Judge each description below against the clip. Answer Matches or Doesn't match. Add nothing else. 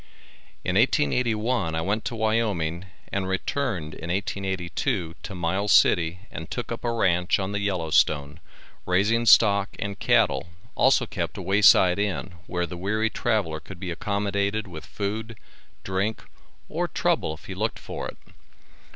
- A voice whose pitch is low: Matches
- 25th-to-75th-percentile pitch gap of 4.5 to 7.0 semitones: Doesn't match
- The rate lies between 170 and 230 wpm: Doesn't match